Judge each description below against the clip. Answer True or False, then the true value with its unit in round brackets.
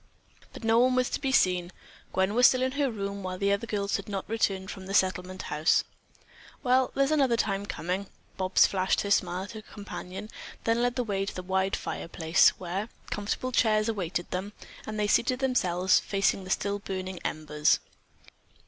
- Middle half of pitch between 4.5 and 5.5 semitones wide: False (3.5 semitones)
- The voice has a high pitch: True (200 Hz)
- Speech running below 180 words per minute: False (185 wpm)